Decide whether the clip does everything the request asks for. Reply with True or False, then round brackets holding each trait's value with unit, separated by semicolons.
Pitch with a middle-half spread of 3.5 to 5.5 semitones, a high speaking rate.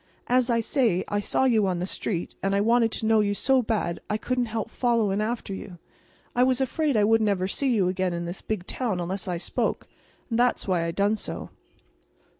True (4.0 semitones; 220 wpm)